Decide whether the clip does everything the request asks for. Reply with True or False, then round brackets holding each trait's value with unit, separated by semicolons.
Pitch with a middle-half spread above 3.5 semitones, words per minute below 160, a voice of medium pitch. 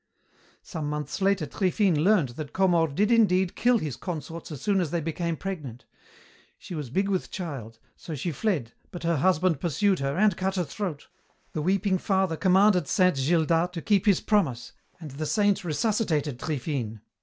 False (4.4 semitones; 175 wpm; 175 Hz)